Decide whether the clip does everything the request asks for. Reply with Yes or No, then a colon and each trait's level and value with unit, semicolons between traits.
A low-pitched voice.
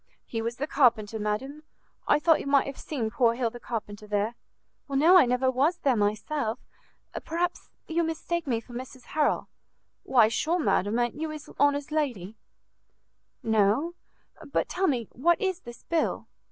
No: very high, 260 Hz